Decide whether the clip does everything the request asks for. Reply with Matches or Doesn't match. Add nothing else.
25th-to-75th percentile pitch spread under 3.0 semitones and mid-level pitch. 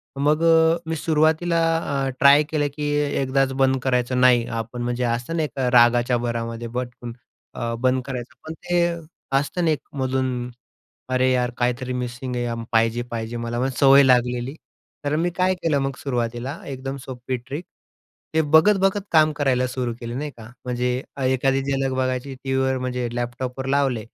Doesn't match